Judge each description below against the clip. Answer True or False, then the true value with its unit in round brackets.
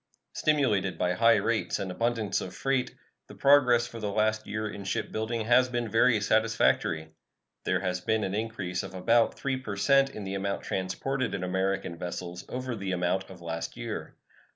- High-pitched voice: False (110 Hz)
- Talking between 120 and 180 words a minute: True (175 wpm)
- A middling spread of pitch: True (4.0 semitones)